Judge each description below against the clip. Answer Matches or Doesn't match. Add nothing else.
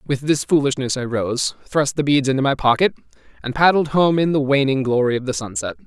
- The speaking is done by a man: Matches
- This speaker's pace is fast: Matches